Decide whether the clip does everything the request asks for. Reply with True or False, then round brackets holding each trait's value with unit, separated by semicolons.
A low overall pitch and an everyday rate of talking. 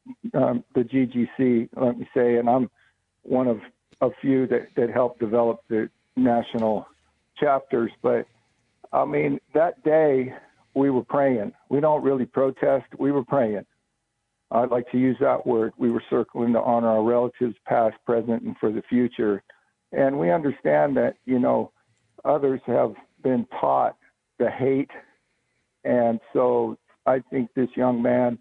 True (125 Hz; 150 wpm)